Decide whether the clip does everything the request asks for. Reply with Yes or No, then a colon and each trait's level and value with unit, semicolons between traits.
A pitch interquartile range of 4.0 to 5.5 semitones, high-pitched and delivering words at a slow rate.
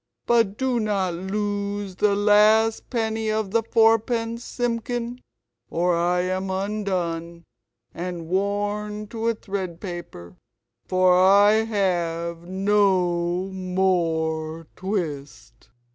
No: average, 3.5 semitones; high, 195 Hz; slow, 100 wpm